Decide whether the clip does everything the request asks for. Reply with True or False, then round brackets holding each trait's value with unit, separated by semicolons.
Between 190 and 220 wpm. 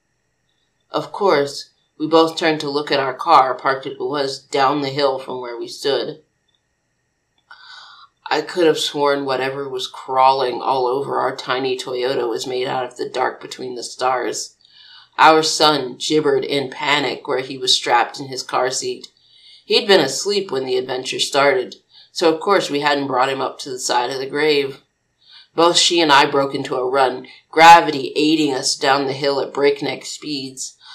False (180 wpm)